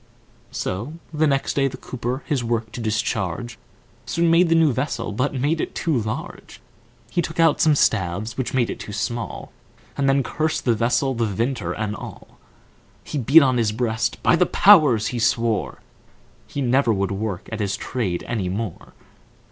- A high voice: No, low, 120 Hz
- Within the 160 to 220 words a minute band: Yes, average, 180 wpm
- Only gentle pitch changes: No, average, 4.5 semitones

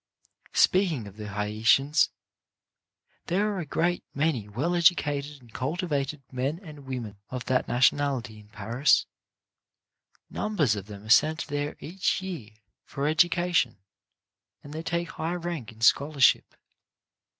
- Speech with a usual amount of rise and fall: No, wide, 6.1 semitones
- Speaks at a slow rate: Yes, slow, 130 wpm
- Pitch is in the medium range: Yes, medium, 145 Hz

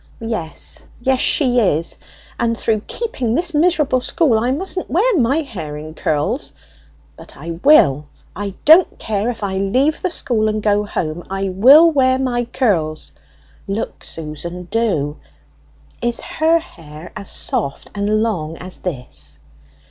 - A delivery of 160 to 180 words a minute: No, average, 145 wpm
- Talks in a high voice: Yes, high, 215 Hz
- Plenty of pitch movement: Yes, wide, 7.8 semitones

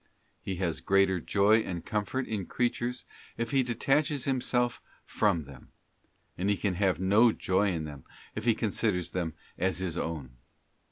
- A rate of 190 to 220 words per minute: No, average, 160 wpm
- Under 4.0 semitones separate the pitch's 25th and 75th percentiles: No, average, 5.2 semitones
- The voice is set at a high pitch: No, low, 100 Hz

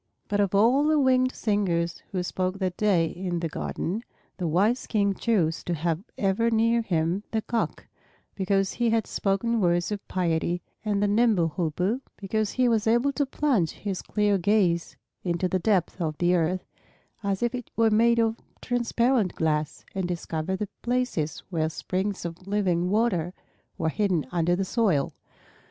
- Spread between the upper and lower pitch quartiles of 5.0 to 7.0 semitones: No, average, 4.5 semitones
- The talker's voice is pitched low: No, high, 195 Hz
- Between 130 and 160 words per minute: No, average, 170 wpm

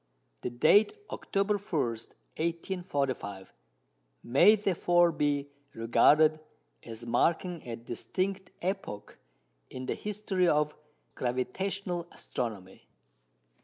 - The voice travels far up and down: Yes, wide, 7.6 semitones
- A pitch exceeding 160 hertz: No, medium, 155 Hz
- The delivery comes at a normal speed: No, slow, 90 wpm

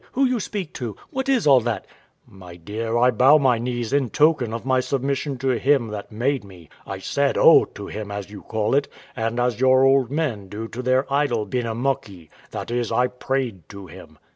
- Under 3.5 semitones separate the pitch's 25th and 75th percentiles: No, average, 4.0 semitones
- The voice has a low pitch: Yes, low, 125 Hz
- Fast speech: Yes, fast, 210 wpm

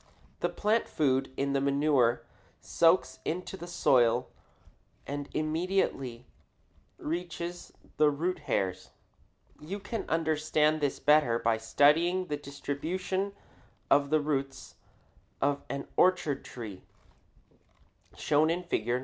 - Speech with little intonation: No, average, 4.0 semitones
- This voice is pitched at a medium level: Yes, medium, 150 Hz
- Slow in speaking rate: Yes, slow, 110 wpm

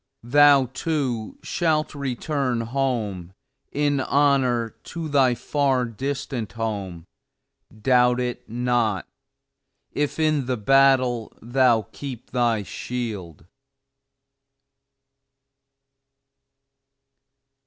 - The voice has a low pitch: Yes, low, 125 Hz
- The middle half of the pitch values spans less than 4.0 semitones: Yes, average, 3.4 semitones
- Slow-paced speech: Yes, slow, 80 wpm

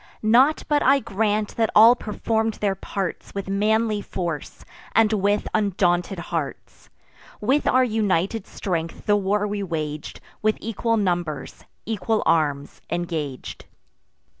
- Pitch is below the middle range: No, high, 205 Hz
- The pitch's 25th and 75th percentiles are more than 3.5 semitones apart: Yes, average, 4.1 semitones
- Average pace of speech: No, slow, 125 wpm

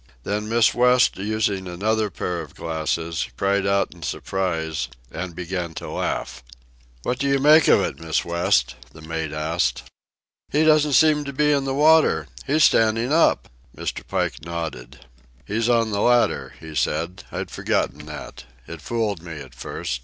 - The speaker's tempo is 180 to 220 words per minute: No, average, 165 wpm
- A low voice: Yes, low, 100 Hz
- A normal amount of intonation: No, wide, 7.0 semitones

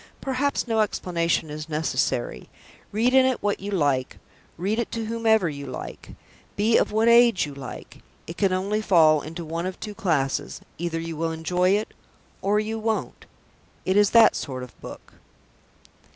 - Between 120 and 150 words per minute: No, average, 170 wpm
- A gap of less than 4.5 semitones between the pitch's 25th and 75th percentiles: No, wide, 5.4 semitones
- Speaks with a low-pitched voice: No, high, 190 Hz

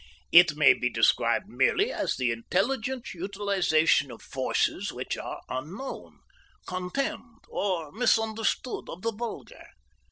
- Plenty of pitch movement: Yes, wide, 6.4 semitones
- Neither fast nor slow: No, slow, 120 wpm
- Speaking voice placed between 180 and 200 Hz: Yes, high, 190 Hz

